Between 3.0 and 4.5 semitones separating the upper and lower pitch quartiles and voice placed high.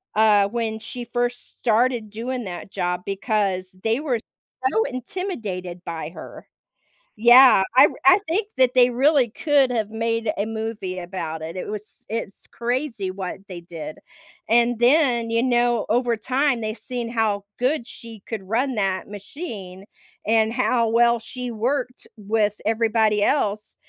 Yes: average, 3.4 semitones; high, 225 Hz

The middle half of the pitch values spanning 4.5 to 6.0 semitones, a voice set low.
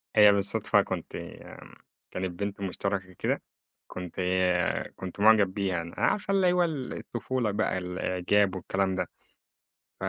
No: average, 2.9 semitones; low, 100 Hz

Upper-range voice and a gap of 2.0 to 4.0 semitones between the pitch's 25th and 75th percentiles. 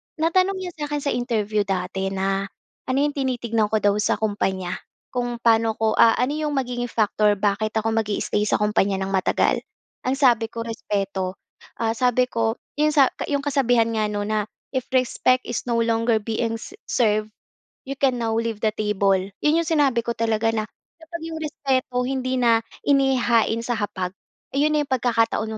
Yes: high, 230 Hz; average, 3.5 semitones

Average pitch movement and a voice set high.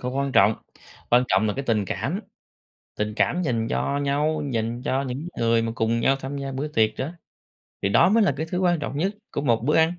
No: average, 4.7 semitones; low, 135 Hz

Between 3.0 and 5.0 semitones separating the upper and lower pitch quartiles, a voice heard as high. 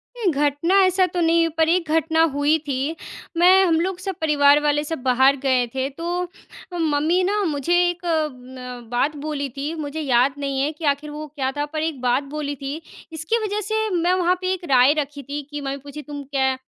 Yes: average, 3.4 semitones; very high, 300 Hz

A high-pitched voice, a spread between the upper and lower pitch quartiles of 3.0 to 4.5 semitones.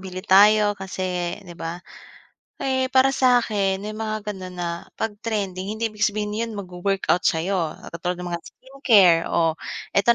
Yes: high, 195 Hz; average, 3.3 semitones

